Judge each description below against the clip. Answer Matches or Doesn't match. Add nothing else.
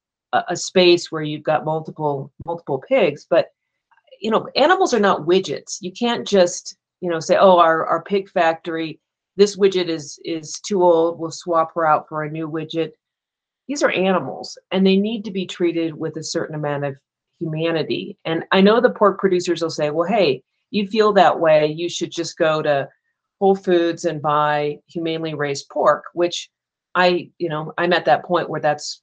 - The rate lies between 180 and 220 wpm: Matches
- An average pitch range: Matches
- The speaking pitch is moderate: Matches